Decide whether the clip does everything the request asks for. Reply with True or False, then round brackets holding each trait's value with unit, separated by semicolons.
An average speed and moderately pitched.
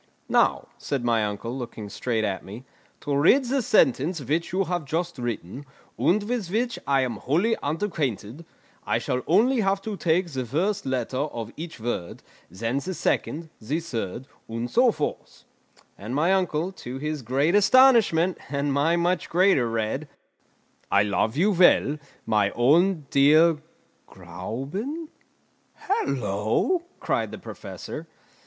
True (145 wpm; 150 Hz)